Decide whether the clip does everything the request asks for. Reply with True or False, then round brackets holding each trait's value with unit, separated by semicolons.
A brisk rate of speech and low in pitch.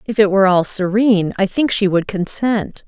False (210 wpm; 200 Hz)